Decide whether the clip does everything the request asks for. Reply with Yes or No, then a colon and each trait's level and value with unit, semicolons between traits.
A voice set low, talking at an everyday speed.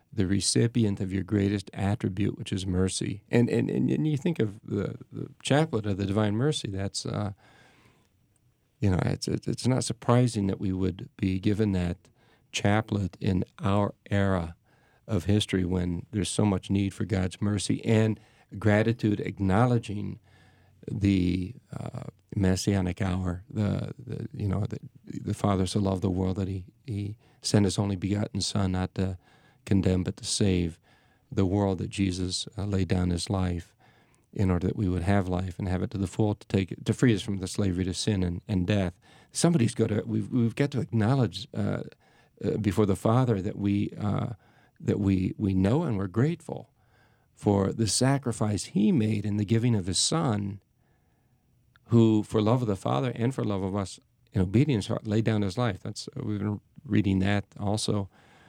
Yes: low, 105 Hz; average, 180 wpm